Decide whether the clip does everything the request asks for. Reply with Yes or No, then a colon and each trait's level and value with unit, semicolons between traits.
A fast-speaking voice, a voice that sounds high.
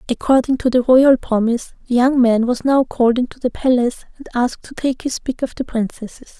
Yes: fast, 215 wpm; high, 245 Hz